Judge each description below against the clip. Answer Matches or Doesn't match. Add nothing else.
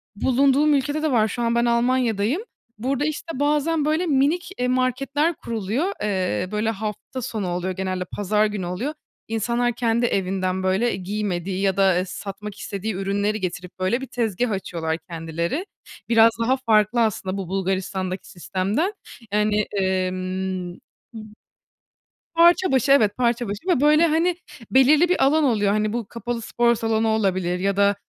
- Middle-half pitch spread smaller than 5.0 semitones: Doesn't match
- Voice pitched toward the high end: Matches